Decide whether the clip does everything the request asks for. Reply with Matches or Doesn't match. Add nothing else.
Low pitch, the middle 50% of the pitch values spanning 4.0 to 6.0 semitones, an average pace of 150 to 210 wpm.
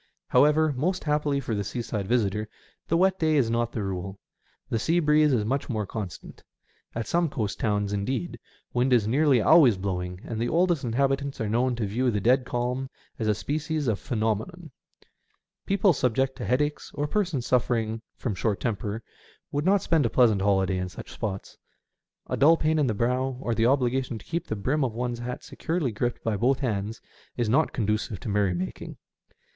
Matches